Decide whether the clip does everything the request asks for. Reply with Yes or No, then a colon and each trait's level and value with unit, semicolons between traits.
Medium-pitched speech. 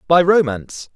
Yes: medium, 160 Hz